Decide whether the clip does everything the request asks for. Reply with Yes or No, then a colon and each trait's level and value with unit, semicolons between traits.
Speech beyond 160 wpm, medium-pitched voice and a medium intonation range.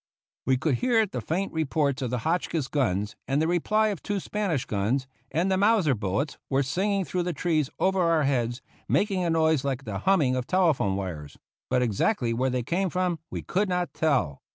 No: average, 200 wpm; medium, 155 Hz; wide, 6.3 semitones